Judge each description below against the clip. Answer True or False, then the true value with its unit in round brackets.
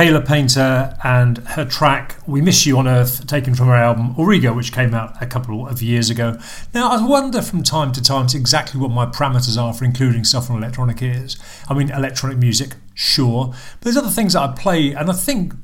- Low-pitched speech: True (130 Hz)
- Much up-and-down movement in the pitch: False (3.5 semitones)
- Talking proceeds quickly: True (215 wpm)